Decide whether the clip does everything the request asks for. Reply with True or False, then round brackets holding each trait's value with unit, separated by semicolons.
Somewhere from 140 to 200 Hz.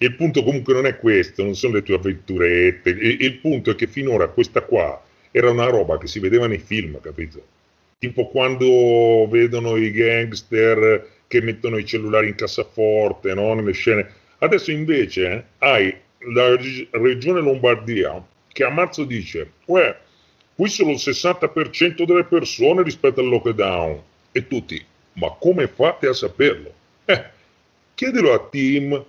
False (125 Hz)